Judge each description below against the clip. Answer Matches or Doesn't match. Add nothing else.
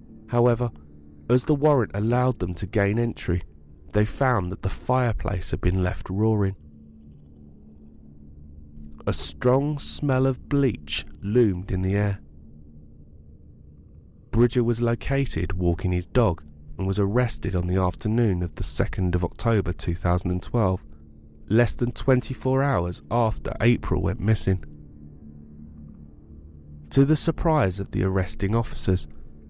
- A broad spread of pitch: Matches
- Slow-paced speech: Matches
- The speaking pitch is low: Matches